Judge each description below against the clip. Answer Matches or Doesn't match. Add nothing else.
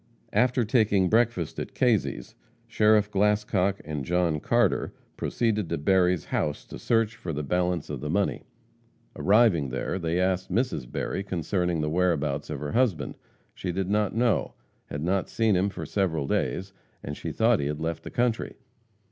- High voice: Doesn't match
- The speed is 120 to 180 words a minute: Matches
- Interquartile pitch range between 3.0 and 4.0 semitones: Doesn't match